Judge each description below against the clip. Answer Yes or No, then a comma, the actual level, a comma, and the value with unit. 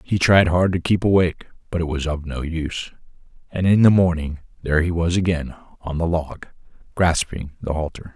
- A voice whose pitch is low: Yes, very low, 85 Hz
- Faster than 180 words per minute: Yes, average, 190 wpm